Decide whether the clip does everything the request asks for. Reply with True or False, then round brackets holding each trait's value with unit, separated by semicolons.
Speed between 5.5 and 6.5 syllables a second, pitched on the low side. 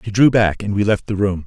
True (5.8 syllables/s; 100 Hz)